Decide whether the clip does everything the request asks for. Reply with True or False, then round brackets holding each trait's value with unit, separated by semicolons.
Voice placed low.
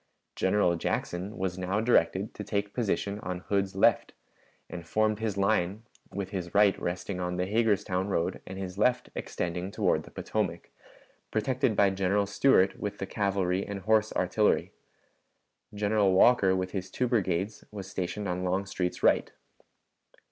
True (100 Hz)